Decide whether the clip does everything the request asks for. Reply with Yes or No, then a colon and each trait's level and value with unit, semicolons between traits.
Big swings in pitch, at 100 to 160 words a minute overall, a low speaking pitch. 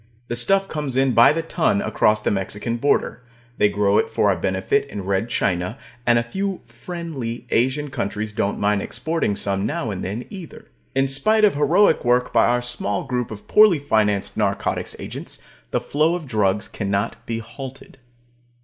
No: wide, 6.1 semitones; average, 175 wpm; low, 120 Hz